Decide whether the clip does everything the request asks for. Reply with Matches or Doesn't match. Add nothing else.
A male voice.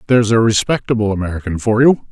Matches